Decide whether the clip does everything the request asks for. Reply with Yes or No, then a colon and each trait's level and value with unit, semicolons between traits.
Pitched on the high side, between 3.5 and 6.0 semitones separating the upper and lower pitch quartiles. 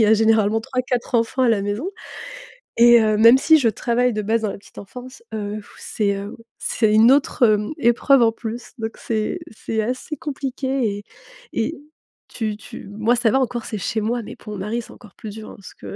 No: high, 225 Hz; narrow, 2.6 semitones